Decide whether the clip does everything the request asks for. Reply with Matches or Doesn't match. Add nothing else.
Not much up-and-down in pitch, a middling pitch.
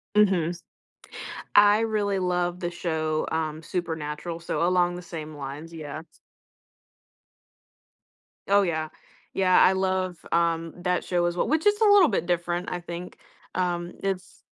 Matches